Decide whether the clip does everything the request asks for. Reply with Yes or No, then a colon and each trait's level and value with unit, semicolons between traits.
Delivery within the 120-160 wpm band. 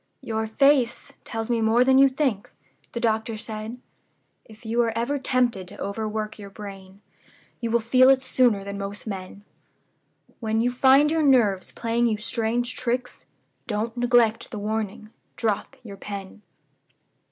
Yes: average, 150 wpm